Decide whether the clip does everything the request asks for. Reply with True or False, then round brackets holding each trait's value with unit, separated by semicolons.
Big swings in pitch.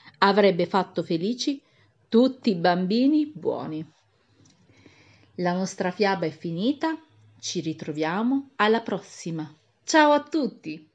True (6.9 semitones)